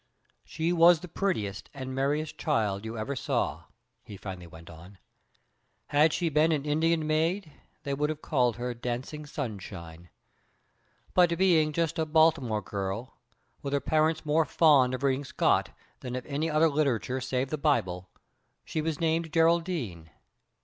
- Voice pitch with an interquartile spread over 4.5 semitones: Yes, average, 5.1 semitones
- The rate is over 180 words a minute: No, average, 155 wpm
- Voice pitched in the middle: Yes, medium, 145 Hz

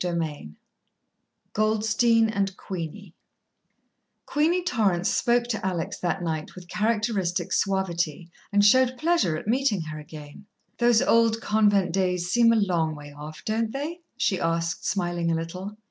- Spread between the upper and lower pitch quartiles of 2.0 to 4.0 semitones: No, average, 4.9 semitones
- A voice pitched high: Yes, high, 195 Hz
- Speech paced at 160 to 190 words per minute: No, average, 140 wpm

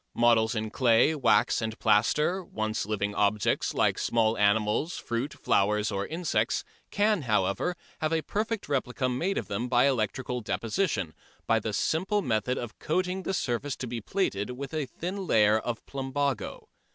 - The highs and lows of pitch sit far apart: Yes, wide, 6.3 semitones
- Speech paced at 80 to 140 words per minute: No, average, 160 wpm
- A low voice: Yes, low, 125 Hz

